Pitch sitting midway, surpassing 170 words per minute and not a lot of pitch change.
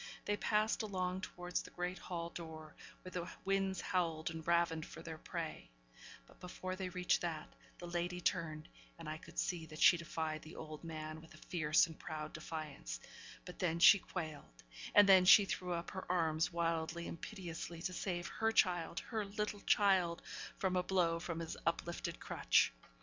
Yes: medium, 170 Hz; average, 180 wpm; narrow, 2.3 semitones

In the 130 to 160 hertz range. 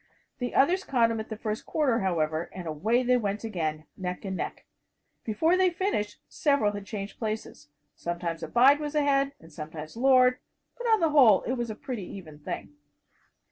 No: high, 220 Hz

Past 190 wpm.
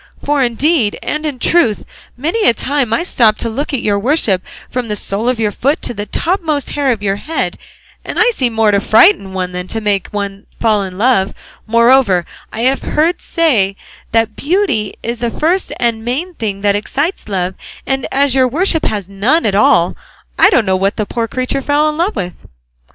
Yes: average, 200 wpm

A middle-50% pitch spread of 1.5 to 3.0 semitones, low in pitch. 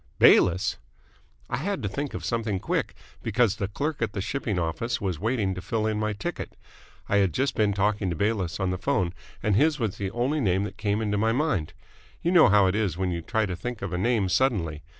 No: average, 3.7 semitones; low, 105 Hz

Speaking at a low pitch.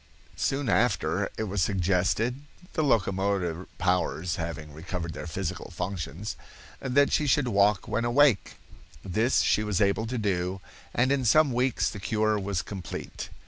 Yes: low, 100 Hz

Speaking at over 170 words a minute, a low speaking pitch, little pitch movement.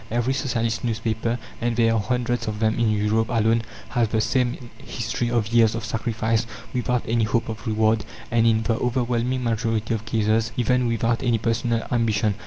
Yes: average, 180 wpm; low, 115 Hz; narrow, 1.3 semitones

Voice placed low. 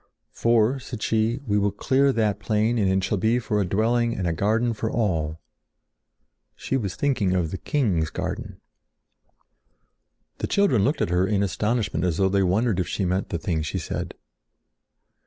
Yes: low, 105 Hz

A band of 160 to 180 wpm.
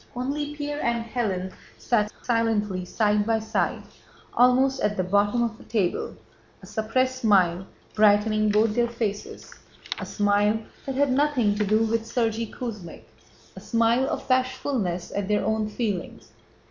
No: average, 145 wpm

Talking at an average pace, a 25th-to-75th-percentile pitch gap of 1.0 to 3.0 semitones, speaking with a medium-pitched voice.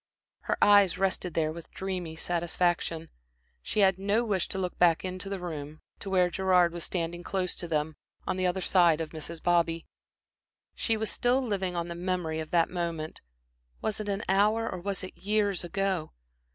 Yes: average, 185 wpm; narrow, 2.6 semitones; medium, 180 Hz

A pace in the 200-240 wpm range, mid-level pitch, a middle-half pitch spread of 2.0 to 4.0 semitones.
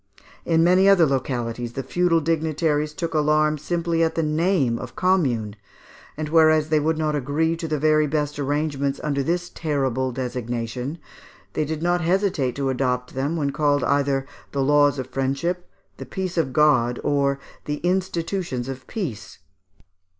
No: average, 155 wpm; medium, 150 Hz; average, 3.5 semitones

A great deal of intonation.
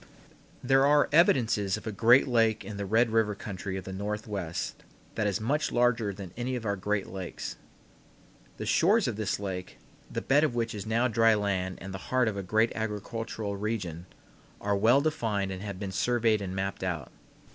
No: average, 2.9 semitones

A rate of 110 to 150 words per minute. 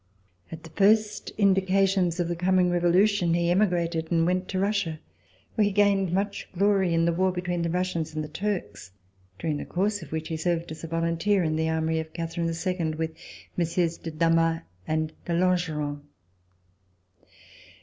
No: average, 170 wpm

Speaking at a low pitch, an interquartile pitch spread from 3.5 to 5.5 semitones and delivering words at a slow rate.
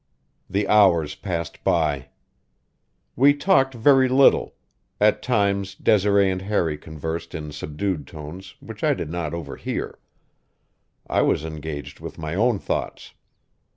Yes: very low, 95 Hz; average, 5.1 semitones; slow, 125 wpm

